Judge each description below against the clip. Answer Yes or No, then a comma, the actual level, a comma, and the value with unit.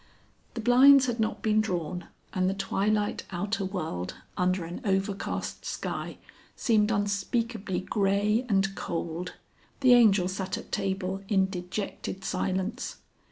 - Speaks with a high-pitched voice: Yes, high, 195 Hz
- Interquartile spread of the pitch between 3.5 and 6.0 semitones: No, narrow, 2.6 semitones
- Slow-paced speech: Yes, slow, 125 wpm